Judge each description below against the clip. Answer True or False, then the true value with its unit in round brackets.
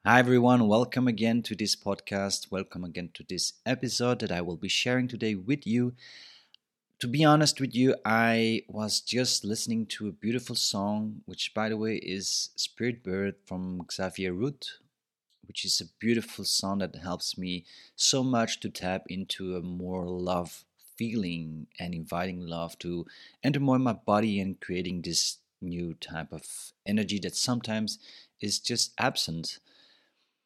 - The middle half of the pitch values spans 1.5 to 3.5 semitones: False (4.9 semitones)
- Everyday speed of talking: True (160 wpm)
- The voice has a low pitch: True (105 Hz)